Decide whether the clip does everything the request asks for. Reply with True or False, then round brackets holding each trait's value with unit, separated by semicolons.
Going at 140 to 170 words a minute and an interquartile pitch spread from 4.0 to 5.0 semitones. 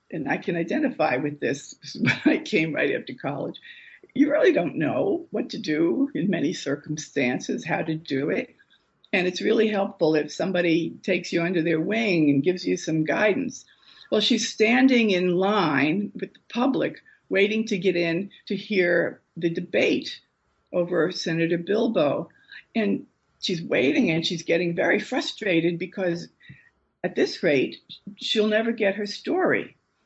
True (160 wpm; 4.7 semitones)